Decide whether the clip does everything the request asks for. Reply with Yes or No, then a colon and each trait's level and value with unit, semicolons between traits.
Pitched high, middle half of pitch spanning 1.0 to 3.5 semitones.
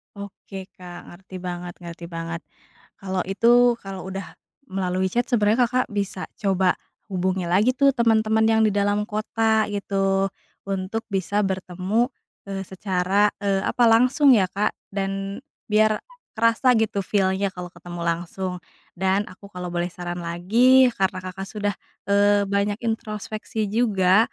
Yes: high, 195 Hz; average, 2.7 semitones